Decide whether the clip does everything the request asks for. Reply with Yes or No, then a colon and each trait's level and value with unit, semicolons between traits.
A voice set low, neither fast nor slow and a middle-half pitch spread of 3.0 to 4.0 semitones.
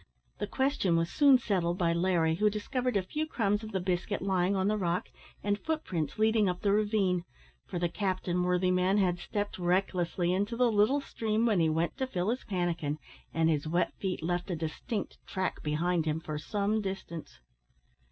No: medium, 185 Hz; average, 190 wpm; average, 3.3 semitones